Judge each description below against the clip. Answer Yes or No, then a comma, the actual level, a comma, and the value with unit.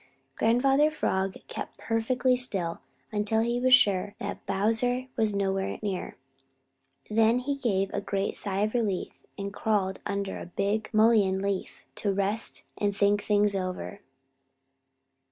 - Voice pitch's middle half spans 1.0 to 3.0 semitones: Yes, narrow, 2.6 semitones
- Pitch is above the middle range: Yes, high, 205 Hz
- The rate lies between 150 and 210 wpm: No, slow, 135 wpm